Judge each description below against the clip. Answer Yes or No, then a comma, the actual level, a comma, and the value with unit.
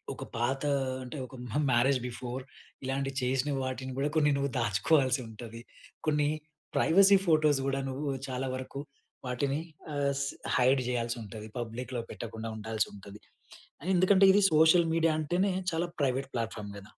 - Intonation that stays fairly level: No, average, 3.8 semitones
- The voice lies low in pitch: Yes, low, 130 Hz